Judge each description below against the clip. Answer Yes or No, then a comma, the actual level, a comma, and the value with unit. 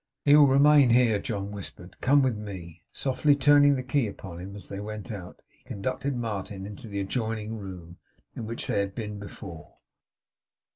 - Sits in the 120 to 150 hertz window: No, low, 105 Hz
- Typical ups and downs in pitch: Yes, average, 4.7 semitones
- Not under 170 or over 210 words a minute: Yes, average, 180 wpm